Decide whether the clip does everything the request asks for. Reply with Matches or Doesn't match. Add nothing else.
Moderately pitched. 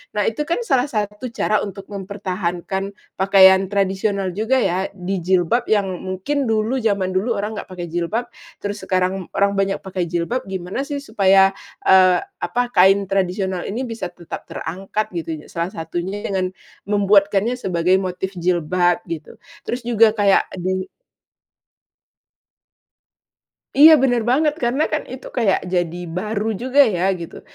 Doesn't match